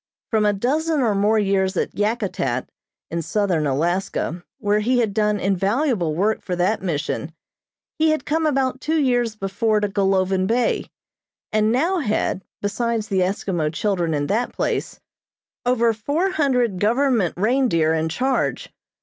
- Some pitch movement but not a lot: Yes, average, 4.8 semitones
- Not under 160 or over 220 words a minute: No, average, 150 wpm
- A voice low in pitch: No, high, 210 Hz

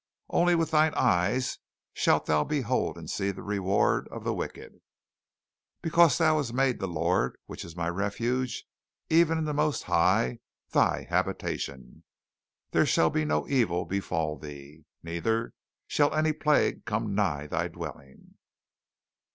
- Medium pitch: No, low, 105 Hz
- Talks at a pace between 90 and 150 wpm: Yes, slow, 135 wpm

